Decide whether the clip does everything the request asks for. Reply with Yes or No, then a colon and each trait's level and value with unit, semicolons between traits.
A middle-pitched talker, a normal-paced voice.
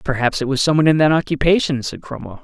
No: medium, 145 Hz; fast, 245 wpm